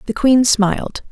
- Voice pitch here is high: Yes, high, 230 Hz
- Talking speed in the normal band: Yes, average, 160 wpm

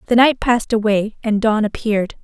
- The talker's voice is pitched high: Yes, high, 220 Hz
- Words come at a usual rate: Yes, average, 190 wpm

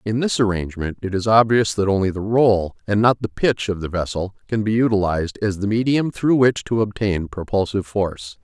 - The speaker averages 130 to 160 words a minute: No, fast, 205 wpm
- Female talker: No, male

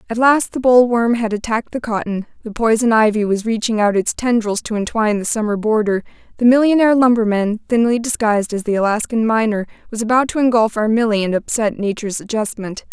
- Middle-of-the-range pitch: No, high, 220 Hz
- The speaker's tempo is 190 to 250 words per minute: No, average, 175 wpm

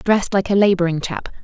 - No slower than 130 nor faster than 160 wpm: No, fast, 210 wpm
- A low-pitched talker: No, medium, 185 Hz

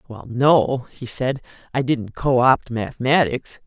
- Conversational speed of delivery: Yes, average, 145 wpm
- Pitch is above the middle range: No, low, 130 Hz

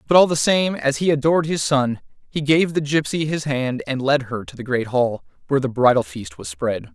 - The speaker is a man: Yes, male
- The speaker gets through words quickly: Yes, fast, 240 wpm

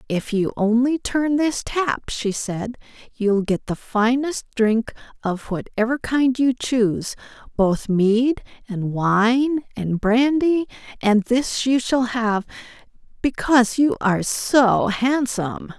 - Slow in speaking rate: Yes, slow, 130 wpm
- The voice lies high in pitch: Yes, high, 235 Hz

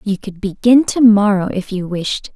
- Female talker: Yes, female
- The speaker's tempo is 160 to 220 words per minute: Yes, fast, 205 wpm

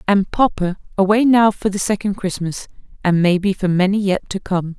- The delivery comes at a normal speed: Yes, average, 190 wpm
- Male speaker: No, female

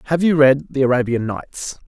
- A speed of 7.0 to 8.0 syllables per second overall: No, 5.2 syllables/s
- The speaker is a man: Yes, male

